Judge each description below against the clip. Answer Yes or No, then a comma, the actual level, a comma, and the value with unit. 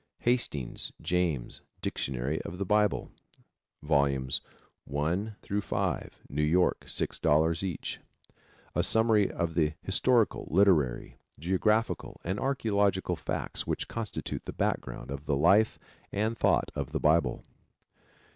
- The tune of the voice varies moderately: No, wide, 5.8 semitones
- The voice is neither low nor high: No, very low, 90 Hz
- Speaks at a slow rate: Yes, slow, 115 wpm